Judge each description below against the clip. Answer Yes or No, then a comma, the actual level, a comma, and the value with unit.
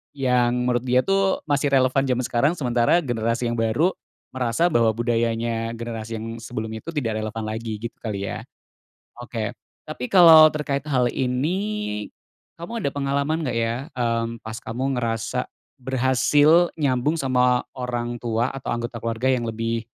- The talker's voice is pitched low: Yes, low, 125 Hz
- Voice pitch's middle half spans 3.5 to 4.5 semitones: No, average, 3.1 semitones